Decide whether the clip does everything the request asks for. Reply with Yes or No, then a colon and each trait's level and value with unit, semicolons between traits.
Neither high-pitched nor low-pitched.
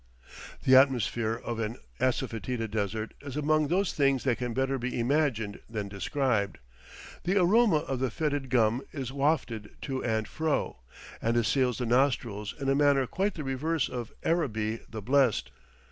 No: low, 130 Hz